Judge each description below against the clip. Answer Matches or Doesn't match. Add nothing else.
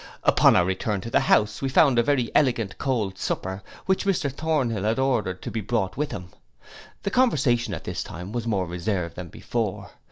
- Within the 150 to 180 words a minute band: Doesn't match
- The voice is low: Matches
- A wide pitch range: Matches